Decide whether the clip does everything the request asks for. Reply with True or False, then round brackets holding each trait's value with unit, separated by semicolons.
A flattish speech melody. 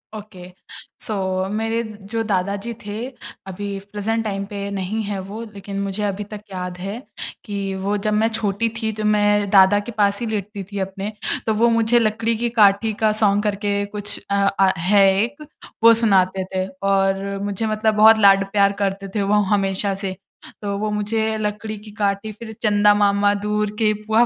True (1.6 semitones)